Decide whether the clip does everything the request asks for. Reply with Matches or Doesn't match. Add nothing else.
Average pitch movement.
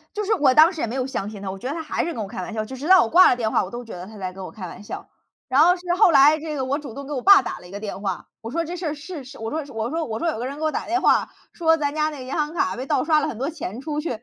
Doesn't match